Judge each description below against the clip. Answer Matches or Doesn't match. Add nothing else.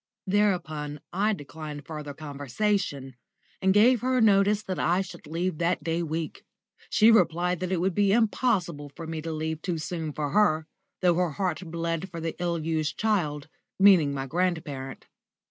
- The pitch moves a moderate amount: Matches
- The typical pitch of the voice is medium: Matches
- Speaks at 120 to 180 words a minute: Matches